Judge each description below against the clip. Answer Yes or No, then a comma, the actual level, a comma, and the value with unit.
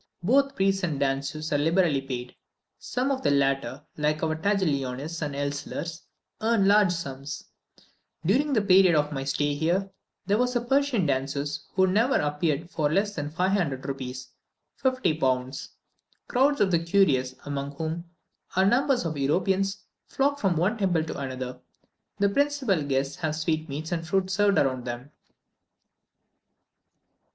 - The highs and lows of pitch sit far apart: Yes, wide, 5.9 semitones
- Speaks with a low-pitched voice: No, medium, 165 Hz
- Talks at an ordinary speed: Yes, average, 150 wpm